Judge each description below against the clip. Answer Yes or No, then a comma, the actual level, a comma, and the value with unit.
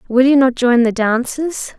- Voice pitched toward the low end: No, very high, 255 Hz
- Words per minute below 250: Yes, average, 200 wpm